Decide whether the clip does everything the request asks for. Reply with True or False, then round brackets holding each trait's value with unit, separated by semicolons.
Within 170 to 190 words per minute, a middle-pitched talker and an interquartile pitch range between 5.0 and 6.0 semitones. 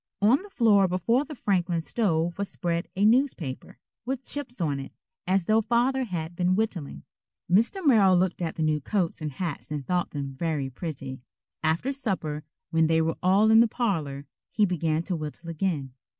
True (180 wpm; 180 Hz; 5.6 semitones)